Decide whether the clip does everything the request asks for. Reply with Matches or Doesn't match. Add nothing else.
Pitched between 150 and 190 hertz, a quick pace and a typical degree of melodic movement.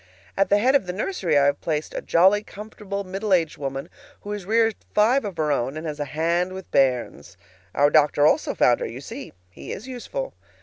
Doesn't match